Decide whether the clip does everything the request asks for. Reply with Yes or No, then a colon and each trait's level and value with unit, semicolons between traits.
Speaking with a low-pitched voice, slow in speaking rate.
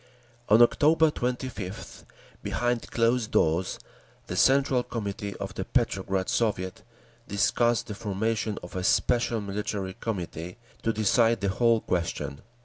Yes: low, 110 Hz; slow, 125 wpm